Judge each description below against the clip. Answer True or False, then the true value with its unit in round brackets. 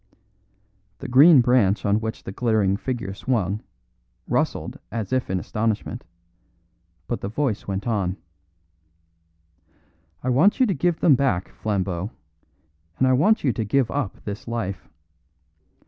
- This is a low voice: True (115 Hz)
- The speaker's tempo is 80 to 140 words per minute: True (135 wpm)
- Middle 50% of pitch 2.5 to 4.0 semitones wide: False (4.7 semitones)